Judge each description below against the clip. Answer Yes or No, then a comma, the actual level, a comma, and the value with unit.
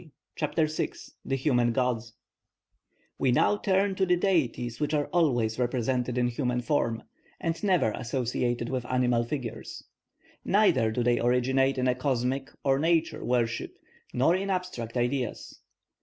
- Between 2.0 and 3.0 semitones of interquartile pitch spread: No, average, 4.1 semitones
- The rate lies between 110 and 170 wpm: Yes, average, 140 wpm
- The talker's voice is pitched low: Yes, low, 130 Hz